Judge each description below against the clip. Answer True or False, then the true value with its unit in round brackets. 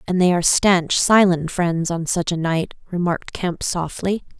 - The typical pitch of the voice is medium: True (175 Hz)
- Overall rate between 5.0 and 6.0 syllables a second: False (4.5 syllables/s)